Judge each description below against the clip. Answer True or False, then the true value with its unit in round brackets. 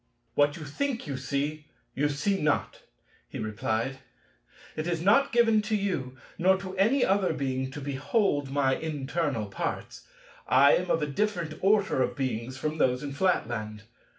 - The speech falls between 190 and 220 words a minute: False (160 wpm)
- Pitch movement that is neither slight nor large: False (6.2 semitones)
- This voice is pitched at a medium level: True (145 Hz)